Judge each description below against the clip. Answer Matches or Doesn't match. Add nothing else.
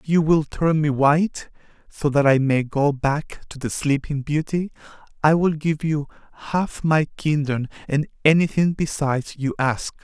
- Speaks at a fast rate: Doesn't match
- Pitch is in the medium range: Matches